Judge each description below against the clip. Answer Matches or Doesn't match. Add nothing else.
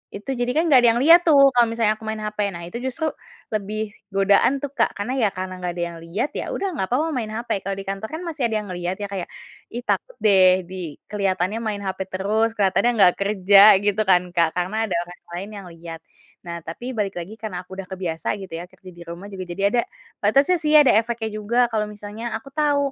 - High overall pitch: Matches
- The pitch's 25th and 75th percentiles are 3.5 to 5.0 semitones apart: Matches